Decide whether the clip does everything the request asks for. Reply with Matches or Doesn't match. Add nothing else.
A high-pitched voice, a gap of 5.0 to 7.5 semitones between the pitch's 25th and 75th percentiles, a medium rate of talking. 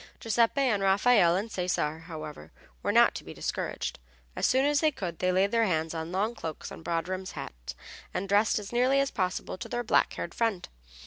Doesn't match